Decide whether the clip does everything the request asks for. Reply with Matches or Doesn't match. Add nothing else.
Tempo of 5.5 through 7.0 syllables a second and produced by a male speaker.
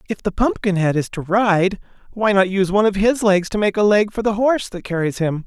Matches